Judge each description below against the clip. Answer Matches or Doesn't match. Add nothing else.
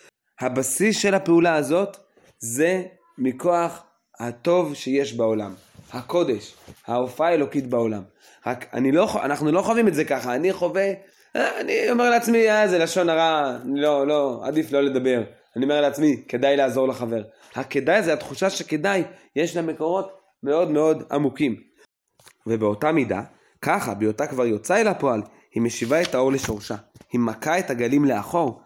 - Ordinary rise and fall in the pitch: Doesn't match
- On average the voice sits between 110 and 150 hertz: Matches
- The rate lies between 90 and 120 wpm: Doesn't match